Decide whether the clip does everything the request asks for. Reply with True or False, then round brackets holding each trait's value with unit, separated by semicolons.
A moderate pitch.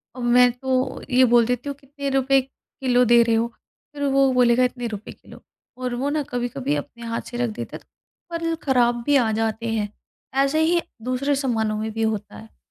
False (245 Hz)